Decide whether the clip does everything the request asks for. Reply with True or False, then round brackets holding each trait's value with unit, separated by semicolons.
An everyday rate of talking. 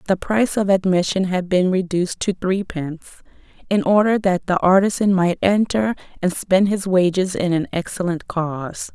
True (160 wpm)